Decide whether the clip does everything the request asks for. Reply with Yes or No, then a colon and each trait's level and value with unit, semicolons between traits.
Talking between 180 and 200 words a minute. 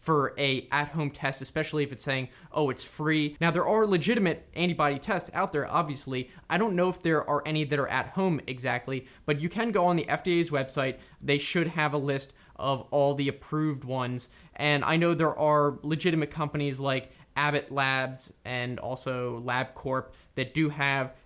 Yes: average, 185 wpm